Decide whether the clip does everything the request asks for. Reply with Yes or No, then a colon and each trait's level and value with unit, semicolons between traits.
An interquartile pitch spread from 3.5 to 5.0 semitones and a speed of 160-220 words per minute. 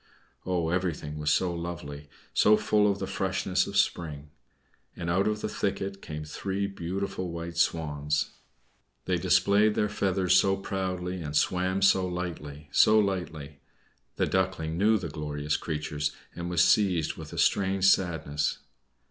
No: average, 4.1 semitones; average, 150 wpm